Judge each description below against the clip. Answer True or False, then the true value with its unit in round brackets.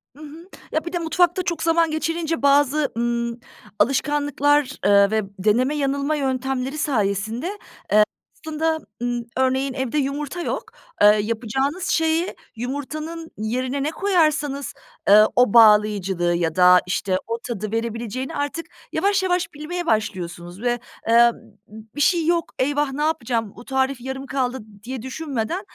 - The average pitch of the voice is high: True (265 Hz)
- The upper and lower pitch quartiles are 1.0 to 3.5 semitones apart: False (5.2 semitones)